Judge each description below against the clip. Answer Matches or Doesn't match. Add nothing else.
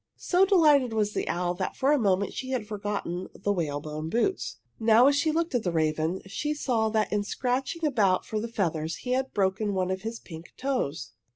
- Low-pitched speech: Doesn't match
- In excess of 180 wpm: Matches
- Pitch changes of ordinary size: Doesn't match